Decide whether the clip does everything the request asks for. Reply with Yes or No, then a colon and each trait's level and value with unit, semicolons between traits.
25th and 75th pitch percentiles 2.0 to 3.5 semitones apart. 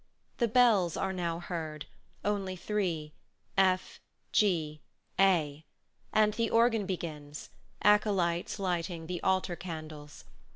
No: average, 4.0 semitones